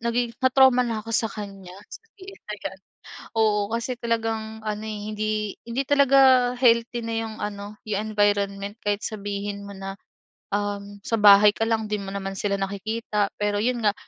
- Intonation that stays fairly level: Yes, narrow, 2.3 semitones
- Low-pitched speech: No, high, 215 Hz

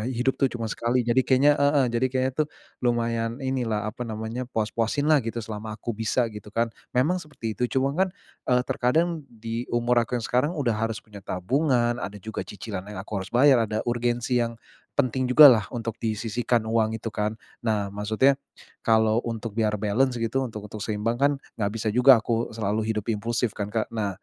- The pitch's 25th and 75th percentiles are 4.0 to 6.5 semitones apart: No, narrow, 2.6 semitones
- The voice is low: Yes, low, 115 Hz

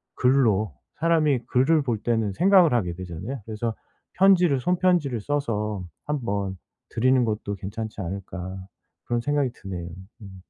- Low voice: Yes, low, 115 Hz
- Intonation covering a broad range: Yes, wide, 6.5 semitones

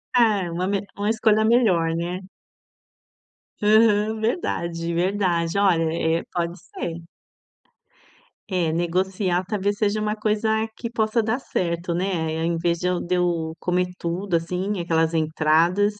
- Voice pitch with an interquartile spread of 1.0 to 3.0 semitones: No, average, 3.6 semitones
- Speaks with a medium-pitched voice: Yes, medium, 180 Hz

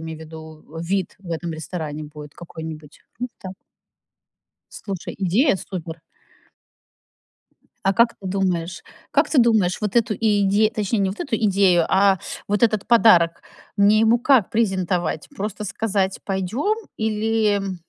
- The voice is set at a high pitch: Yes, high, 195 Hz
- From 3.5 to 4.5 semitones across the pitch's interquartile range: Yes, average, 4.1 semitones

